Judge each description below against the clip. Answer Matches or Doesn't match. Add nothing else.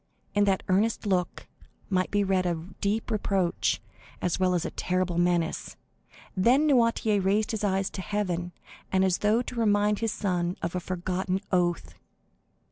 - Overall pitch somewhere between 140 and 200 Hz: Matches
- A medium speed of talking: Matches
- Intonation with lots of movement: Doesn't match